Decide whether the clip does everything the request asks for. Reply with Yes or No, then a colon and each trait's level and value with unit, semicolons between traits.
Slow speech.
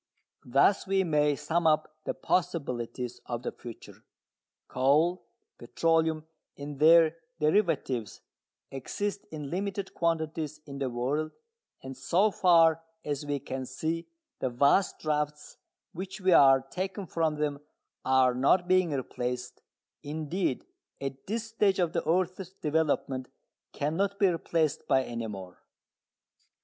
Yes: slow, 125 wpm